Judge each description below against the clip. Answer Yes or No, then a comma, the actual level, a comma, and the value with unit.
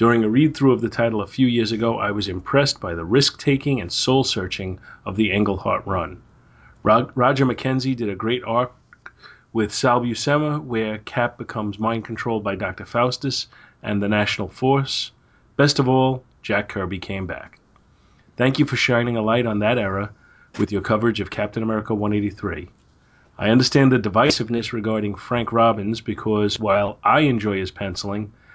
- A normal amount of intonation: Yes, average, 3.3 semitones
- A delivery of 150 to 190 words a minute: Yes, average, 165 wpm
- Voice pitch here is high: No, low, 115 Hz